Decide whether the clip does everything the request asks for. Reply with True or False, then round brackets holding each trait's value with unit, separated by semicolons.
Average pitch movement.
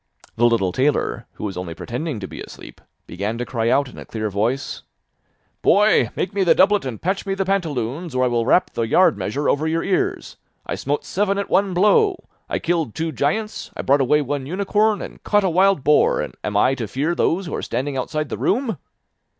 False (8.1 semitones)